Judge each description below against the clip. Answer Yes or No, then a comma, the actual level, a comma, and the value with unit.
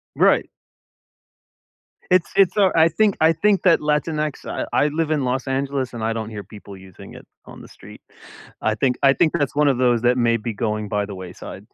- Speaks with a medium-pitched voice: No, low, 130 Hz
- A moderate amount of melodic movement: No, wide, 5.8 semitones